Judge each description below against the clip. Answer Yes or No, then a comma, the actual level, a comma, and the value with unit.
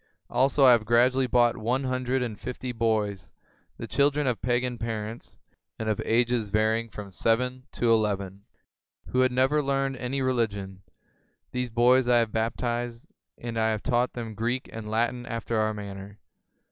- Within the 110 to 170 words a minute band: Yes, average, 165 wpm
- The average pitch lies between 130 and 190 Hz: No, low, 120 Hz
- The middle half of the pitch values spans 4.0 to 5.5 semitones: No, narrow, 2.5 semitones